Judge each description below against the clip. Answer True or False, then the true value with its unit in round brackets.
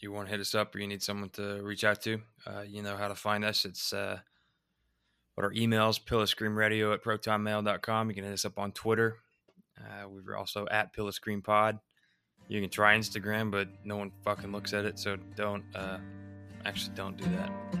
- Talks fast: True (210 wpm)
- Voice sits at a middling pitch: False (105 Hz)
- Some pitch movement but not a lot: False (1.4 semitones)